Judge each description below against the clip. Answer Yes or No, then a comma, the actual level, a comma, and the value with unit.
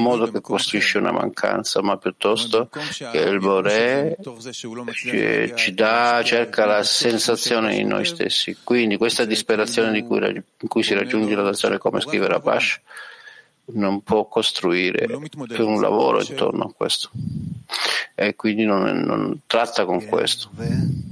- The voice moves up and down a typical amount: No, narrow, 1.9 semitones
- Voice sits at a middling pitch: No, low, 115 Hz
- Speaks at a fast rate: No, average, 140 wpm